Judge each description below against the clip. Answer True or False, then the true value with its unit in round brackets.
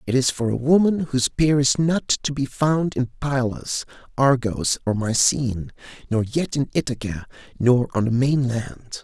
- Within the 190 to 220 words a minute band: False (165 wpm)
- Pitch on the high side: False (130 Hz)